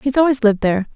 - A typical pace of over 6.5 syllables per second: Yes, 8.1 syllables/s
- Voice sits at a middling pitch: No, high, 240 Hz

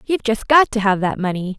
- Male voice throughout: No, female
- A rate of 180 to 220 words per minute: No, fast, 265 wpm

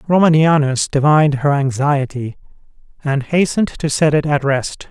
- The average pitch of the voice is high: No, medium, 145 Hz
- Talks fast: No, slow, 135 wpm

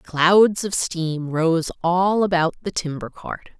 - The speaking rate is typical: Yes, average, 150 wpm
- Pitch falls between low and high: Yes, medium, 170 Hz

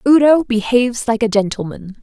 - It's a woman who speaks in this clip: Yes, female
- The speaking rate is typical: Yes, average, 150 wpm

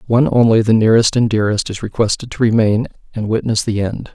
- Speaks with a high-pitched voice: No, low, 110 Hz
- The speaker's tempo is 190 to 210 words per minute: Yes, fast, 205 wpm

